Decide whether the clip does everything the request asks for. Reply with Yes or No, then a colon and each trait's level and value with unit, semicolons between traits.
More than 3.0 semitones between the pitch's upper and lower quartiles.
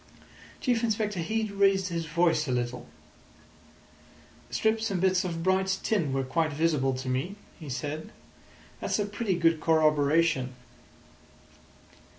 Yes: average, 5.1 semitones